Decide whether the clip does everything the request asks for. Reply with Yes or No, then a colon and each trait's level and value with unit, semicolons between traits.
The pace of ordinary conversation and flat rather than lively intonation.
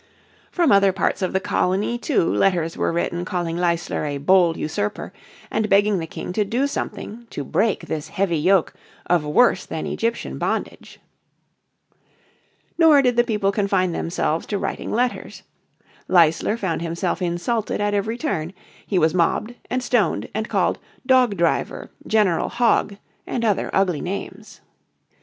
No: average, 150 wpm; average, 4.4 semitones